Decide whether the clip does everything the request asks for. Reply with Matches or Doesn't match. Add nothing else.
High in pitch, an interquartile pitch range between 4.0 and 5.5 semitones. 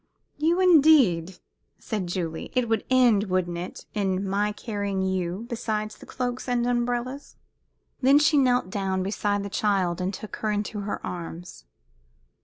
Matches